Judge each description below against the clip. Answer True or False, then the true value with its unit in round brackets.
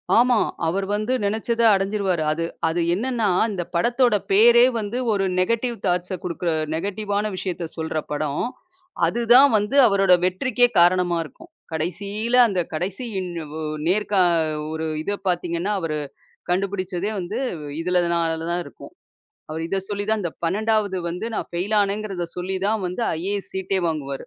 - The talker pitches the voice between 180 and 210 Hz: True (190 Hz)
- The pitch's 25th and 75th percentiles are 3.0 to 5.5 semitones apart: True (3.5 semitones)